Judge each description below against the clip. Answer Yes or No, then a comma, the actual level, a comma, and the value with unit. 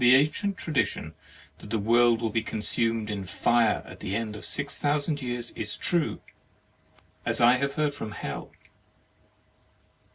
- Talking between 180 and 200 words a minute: No, average, 155 wpm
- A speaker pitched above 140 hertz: No, low, 120 Hz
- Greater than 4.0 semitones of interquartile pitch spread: Yes, average, 4.5 semitones